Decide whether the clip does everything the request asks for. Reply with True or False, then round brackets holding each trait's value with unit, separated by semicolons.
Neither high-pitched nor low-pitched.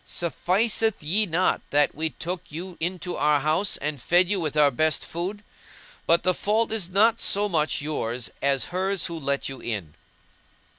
True (170 Hz)